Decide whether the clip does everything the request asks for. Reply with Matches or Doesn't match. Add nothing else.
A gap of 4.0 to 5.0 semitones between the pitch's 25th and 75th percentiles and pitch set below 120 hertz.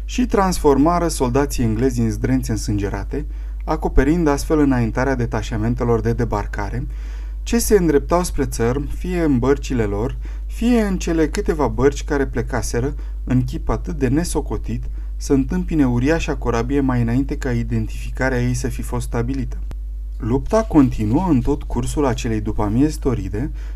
Doesn't match